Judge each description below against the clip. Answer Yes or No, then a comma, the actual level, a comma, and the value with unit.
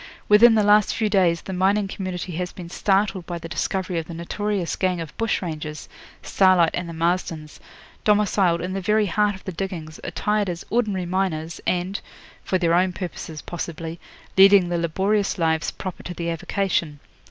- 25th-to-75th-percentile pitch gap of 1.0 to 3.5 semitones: Yes, average, 2.8 semitones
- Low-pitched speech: No, medium, 180 Hz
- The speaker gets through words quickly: No, average, 175 wpm